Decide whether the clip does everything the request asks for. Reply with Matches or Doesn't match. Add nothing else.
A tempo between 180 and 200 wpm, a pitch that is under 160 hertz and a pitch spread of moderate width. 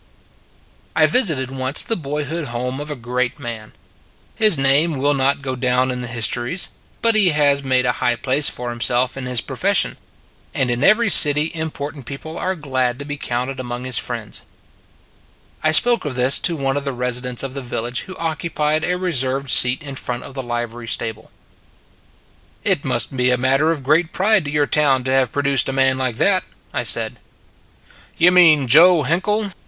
Matches